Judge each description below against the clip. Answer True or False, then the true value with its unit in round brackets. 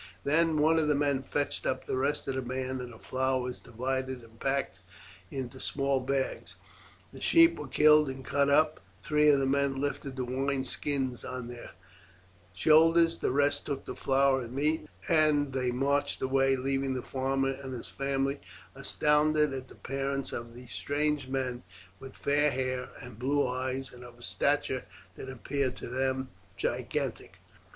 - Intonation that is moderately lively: False (1.8 semitones)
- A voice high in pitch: False (135 Hz)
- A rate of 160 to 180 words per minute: True (175 wpm)